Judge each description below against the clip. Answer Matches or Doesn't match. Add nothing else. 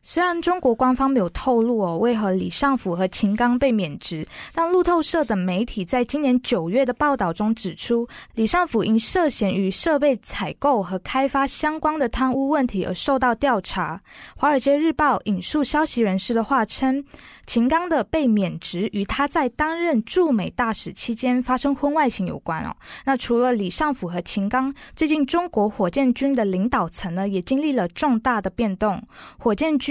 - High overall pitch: Matches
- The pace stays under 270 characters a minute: Doesn't match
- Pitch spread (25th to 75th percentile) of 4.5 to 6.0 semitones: Matches